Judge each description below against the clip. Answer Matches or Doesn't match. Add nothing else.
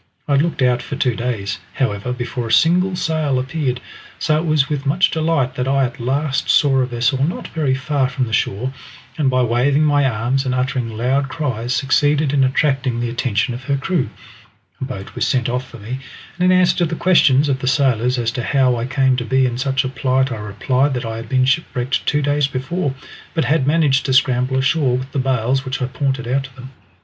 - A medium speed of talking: Doesn't match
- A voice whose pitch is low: Matches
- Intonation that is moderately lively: Doesn't match